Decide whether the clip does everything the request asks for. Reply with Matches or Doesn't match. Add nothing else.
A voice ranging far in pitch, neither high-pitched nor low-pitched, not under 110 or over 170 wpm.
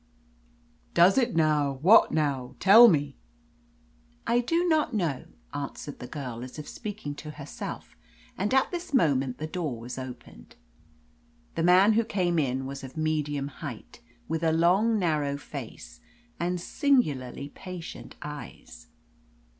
Matches